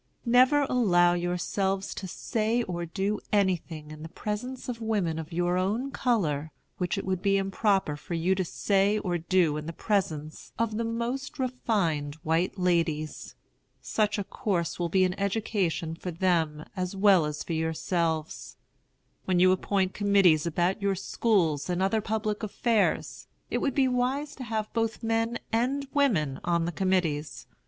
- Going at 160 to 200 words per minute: Yes, average, 165 wpm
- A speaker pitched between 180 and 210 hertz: Yes, high, 190 Hz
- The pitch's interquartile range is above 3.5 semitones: Yes, average, 4.6 semitones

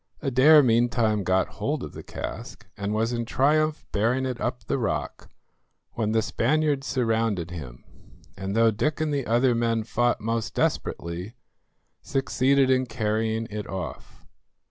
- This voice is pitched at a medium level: No, low, 115 Hz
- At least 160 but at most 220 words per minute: No, average, 145 wpm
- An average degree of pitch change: Yes, average, 3.5 semitones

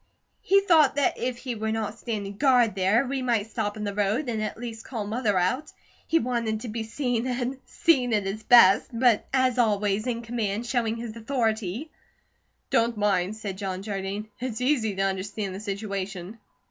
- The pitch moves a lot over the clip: No, average, 3.3 semitones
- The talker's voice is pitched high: Yes, high, 225 Hz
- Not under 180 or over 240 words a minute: Yes, average, 185 wpm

